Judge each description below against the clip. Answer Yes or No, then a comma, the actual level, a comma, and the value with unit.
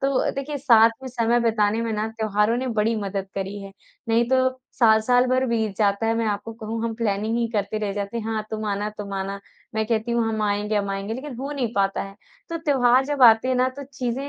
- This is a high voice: Yes, high, 225 Hz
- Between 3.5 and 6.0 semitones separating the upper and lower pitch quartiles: No, average, 3.0 semitones